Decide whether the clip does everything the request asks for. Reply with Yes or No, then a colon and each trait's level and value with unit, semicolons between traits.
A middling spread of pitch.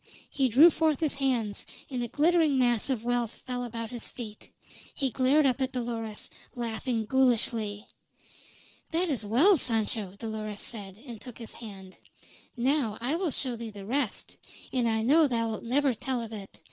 Yes: average, 3.4 semitones